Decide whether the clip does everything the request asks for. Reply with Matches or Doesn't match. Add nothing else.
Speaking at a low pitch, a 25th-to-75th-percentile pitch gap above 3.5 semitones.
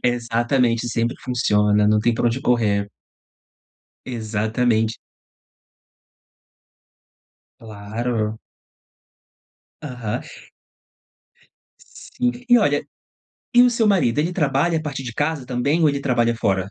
Matches